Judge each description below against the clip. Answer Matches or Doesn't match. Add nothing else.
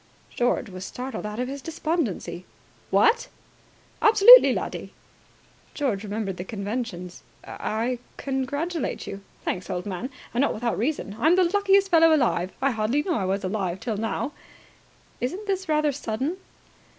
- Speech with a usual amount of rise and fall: Doesn't match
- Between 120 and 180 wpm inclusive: Matches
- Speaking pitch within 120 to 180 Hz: Doesn't match